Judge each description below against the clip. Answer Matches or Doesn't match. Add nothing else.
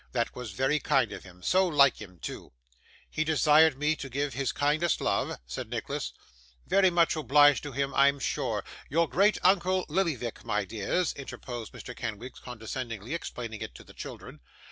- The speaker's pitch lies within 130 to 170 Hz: Matches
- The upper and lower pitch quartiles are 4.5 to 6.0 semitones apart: Matches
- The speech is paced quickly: Doesn't match